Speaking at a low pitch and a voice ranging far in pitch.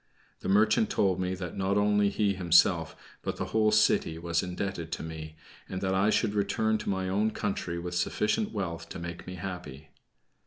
No: very low, 95 Hz; average, 3.2 semitones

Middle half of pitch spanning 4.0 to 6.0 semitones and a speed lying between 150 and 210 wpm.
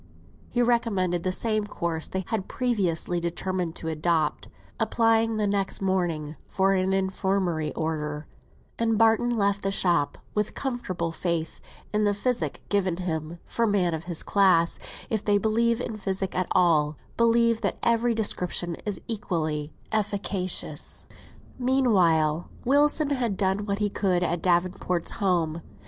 No: average, 4.4 semitones; average, 140 wpm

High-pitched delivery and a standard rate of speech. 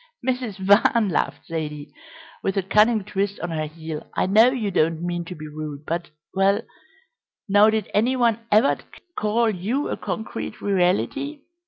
Yes: high, 200 Hz; average, 160 wpm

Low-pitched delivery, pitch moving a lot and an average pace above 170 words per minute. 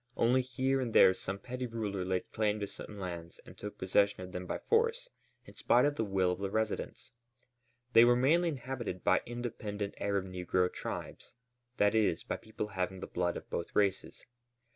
No: low, 105 Hz; average, 4.6 semitones; average, 185 wpm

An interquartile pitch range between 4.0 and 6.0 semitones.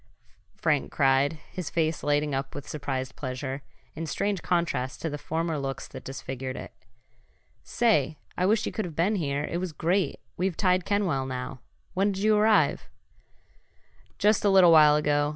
Yes: average, 5.1 semitones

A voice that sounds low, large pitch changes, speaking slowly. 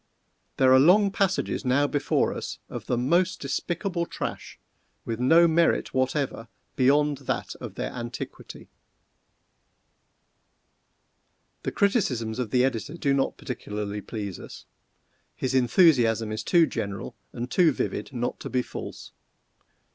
Yes: low, 130 Hz; wide, 5.7 semitones; slow, 130 wpm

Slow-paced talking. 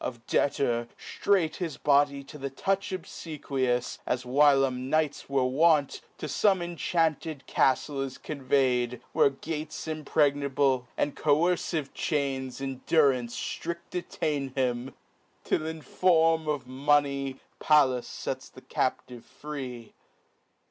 Yes: slow, 120 wpm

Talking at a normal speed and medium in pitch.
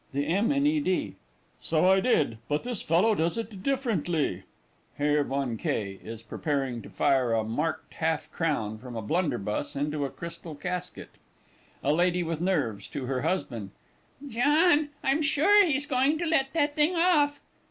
Yes: average, 165 wpm; medium, 165 Hz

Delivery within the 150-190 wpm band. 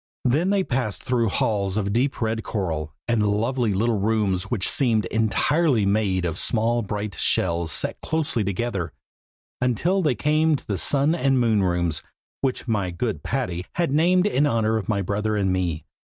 Yes: average, 170 wpm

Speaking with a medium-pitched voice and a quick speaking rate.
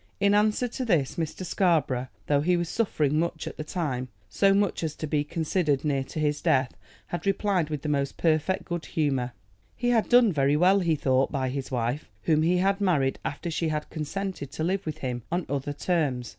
Yes: medium, 155 Hz; fast, 210 wpm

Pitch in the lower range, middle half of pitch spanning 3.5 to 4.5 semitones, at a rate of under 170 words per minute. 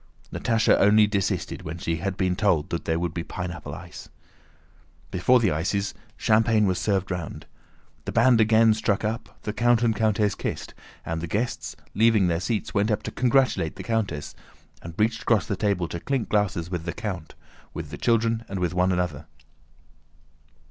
No: low, 100 Hz; average, 4.1 semitones; average, 175 wpm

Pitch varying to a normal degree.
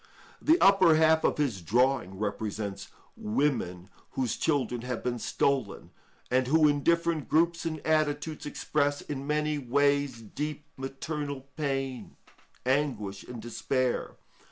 Yes: average, 3.8 semitones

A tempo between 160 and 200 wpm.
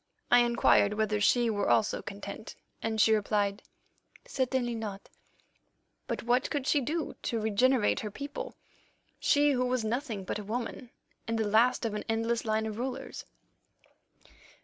No: average, 150 wpm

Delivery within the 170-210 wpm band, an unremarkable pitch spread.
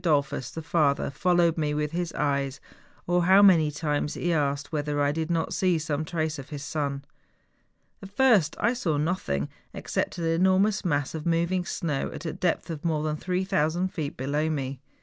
Yes: average, 190 wpm; average, 3.3 semitones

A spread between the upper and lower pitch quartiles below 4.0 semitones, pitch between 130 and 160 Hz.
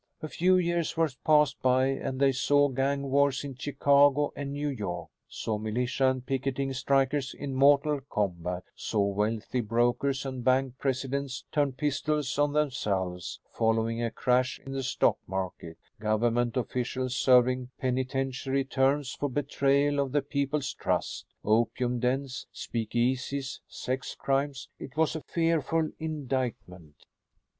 Yes: narrow, 2.6 semitones; low, 135 Hz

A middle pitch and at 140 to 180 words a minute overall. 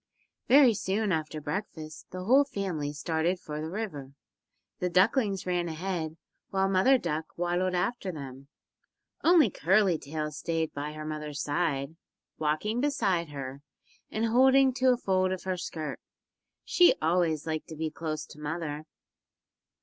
Yes: medium, 170 Hz; average, 145 wpm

